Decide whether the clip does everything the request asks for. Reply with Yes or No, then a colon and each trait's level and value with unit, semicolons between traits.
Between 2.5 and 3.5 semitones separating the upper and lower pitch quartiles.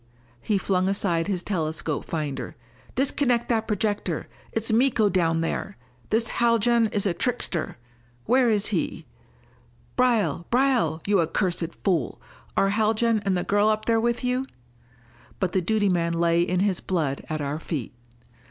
No: average, 5.1 semitones